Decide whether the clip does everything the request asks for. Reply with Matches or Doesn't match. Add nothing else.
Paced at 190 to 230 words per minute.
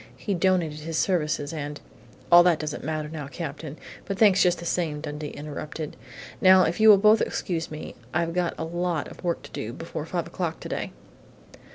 Matches